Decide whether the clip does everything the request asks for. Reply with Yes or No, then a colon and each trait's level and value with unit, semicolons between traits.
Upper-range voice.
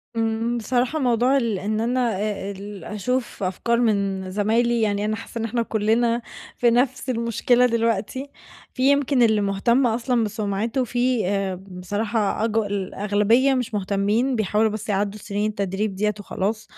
Yes: high, 220 Hz